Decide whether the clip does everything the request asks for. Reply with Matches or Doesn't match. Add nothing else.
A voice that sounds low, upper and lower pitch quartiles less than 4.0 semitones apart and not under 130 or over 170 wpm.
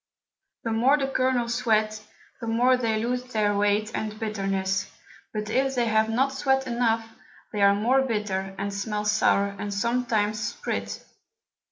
Doesn't match